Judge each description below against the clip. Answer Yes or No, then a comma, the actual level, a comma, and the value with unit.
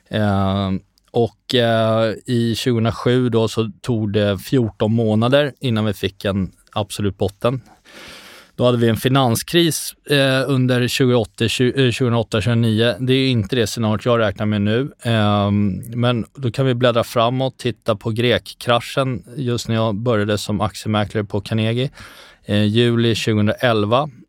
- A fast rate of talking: No, average, 145 wpm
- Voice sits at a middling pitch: No, low, 115 Hz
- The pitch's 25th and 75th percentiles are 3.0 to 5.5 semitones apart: No, narrow, 2.6 semitones